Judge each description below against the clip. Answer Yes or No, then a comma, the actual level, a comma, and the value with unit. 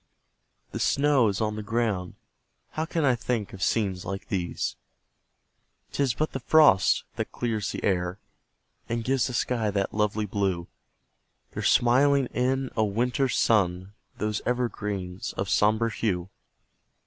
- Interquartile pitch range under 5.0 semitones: Yes, average, 4.2 semitones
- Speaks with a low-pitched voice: Yes, low, 110 Hz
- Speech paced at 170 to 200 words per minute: No, average, 140 wpm